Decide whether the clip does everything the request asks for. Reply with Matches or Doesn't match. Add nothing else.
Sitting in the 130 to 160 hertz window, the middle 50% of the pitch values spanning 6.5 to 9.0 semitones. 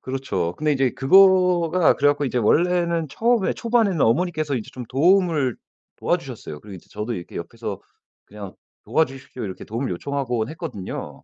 Matches